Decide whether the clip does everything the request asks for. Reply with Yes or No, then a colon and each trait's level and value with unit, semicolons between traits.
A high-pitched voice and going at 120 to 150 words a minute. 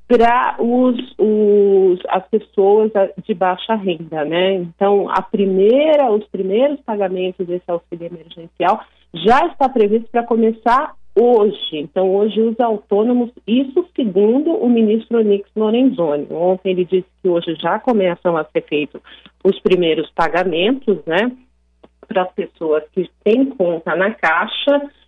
Yes: high, 200 Hz; average, 130 wpm